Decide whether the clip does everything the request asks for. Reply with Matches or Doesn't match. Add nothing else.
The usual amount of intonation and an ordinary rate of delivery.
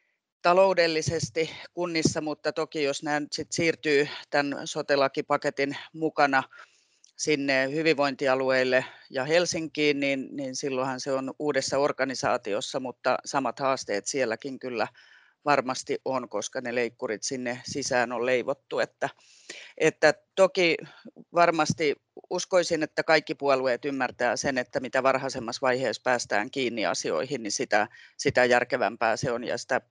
Matches